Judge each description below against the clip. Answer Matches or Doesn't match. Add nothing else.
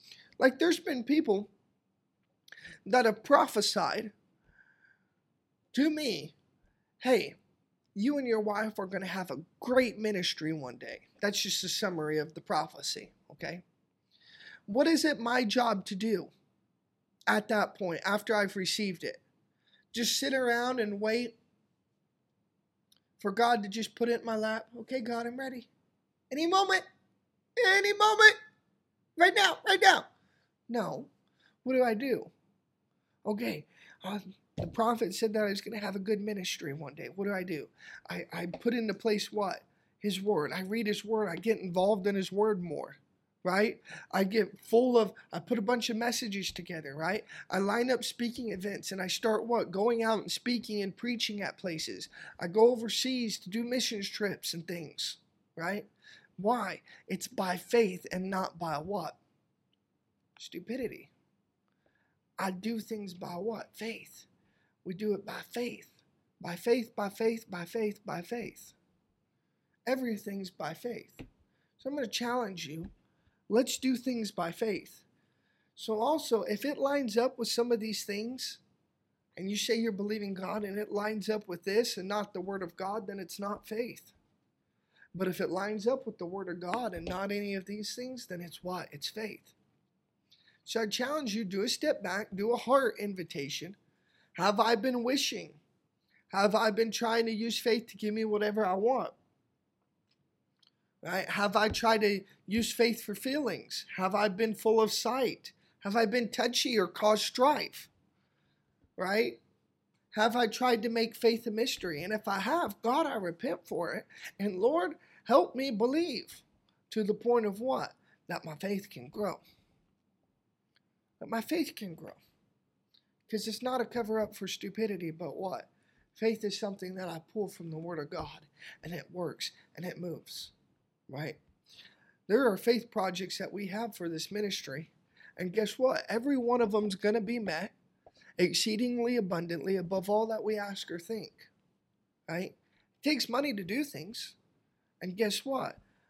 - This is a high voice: Matches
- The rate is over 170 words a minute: Doesn't match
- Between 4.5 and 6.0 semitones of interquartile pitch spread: Doesn't match